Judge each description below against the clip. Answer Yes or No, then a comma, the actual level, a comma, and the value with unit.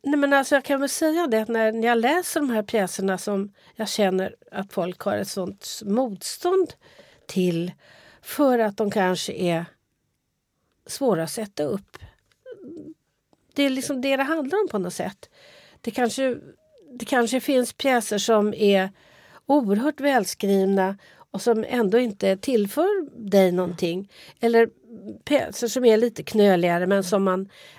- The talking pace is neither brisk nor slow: Yes, average, 150 wpm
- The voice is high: Yes, high, 225 Hz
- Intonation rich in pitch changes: Yes, wide, 5.7 semitones